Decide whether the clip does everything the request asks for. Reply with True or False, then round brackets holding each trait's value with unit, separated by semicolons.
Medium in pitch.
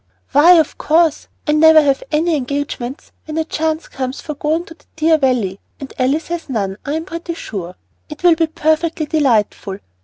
False (305 Hz)